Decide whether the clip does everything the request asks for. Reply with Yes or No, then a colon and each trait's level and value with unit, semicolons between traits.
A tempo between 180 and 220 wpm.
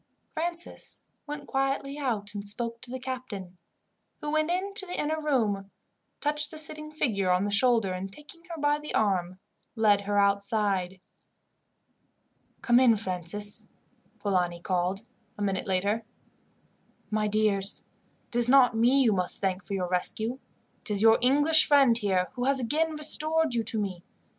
No: average, 160 wpm